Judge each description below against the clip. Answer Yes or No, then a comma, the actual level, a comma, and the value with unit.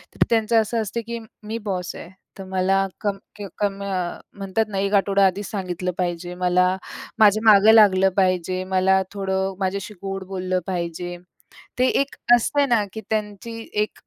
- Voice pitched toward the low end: No, high, 195 Hz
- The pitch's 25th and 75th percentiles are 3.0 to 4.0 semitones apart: No, narrow, 2.4 semitones